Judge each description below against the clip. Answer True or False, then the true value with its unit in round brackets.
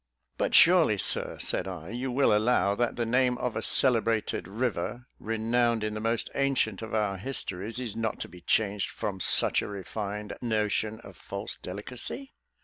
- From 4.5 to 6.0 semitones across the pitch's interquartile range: False (3.1 semitones)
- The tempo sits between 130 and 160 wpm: False (170 wpm)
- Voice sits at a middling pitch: False (110 Hz)